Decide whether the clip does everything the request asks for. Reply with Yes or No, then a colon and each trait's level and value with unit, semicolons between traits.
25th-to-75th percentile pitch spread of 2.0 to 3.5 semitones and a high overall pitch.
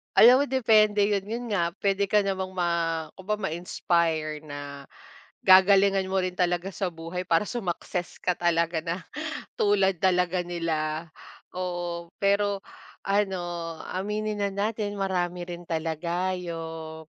No: average, 2.8 semitones; medium, 180 Hz